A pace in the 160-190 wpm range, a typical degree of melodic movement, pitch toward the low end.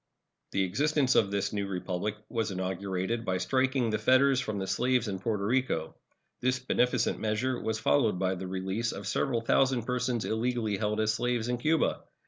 Yes: average, 175 wpm; average, 4.2 semitones; low, 110 Hz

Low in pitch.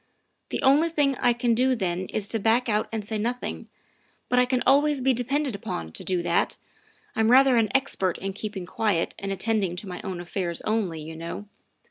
No: high, 220 Hz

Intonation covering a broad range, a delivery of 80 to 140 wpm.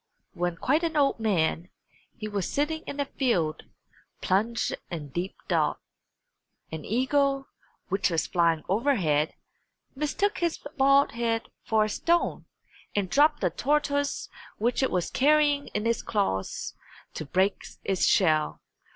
Yes: wide, 8.0 semitones; slow, 135 wpm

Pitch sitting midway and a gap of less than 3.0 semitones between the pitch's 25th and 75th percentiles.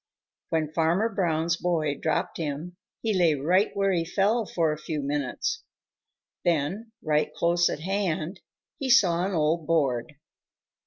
No: medium, 165 Hz; average, 3.6 semitones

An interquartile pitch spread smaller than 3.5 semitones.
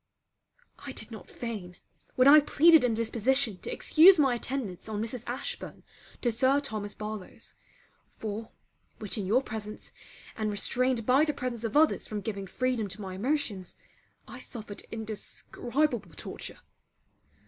No: average, 3.9 semitones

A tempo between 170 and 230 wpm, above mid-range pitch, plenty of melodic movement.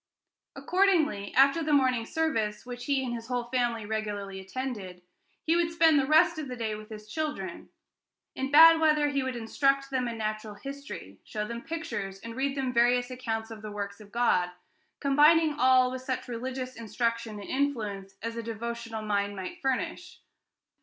No: average, 175 wpm; high, 245 Hz; average, 4.5 semitones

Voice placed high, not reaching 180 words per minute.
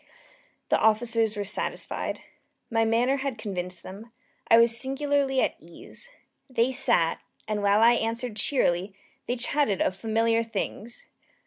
Yes: high, 230 Hz; slow, 135 wpm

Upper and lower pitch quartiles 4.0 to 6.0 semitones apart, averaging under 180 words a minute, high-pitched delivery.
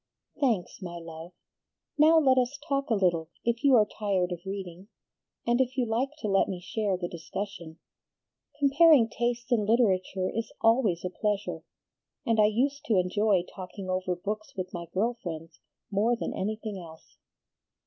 Yes: average, 4.7 semitones; average, 165 wpm; high, 210 Hz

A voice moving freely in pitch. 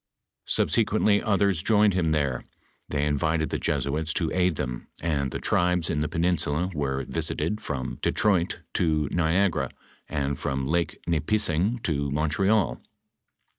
No: average, 4.0 semitones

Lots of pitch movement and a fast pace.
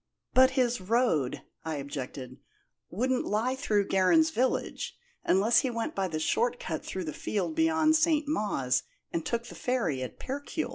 No: wide, 7.6 semitones; average, 160 wpm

